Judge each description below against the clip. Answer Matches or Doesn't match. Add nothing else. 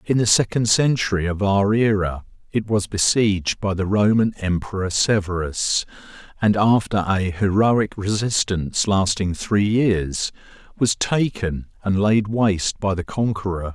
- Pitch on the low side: Matches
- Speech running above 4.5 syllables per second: Doesn't match